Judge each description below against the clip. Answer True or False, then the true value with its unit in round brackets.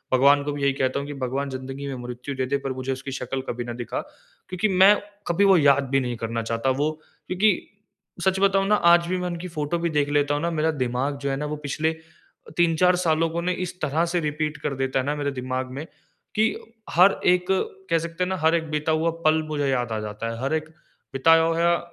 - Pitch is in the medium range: True (150 Hz)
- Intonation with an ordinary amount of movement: True (4.1 semitones)